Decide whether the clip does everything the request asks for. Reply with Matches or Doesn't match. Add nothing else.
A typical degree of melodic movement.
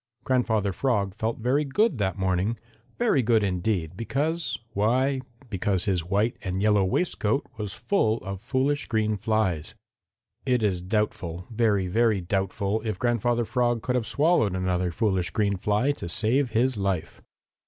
Matches